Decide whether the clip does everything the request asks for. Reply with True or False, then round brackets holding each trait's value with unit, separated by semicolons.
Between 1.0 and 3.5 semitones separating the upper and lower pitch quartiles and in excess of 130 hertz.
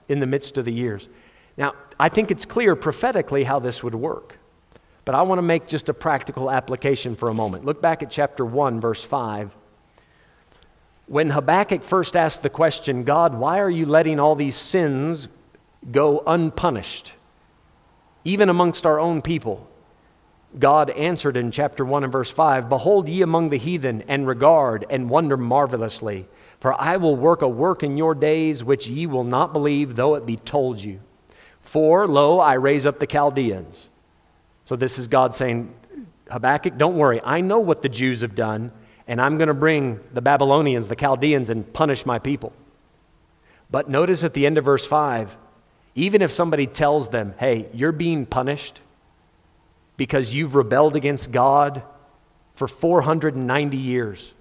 False (4.0 semitones; 140 Hz)